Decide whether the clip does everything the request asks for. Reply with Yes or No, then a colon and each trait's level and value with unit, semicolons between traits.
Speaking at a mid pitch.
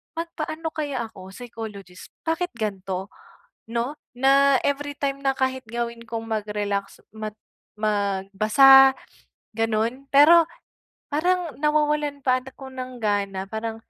No: high, 245 Hz